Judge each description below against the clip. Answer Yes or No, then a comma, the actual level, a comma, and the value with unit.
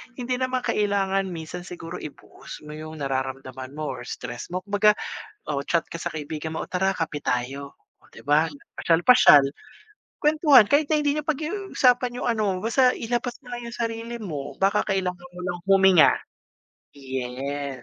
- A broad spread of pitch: Yes, wide, 8.4 semitones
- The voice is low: No, medium, 180 Hz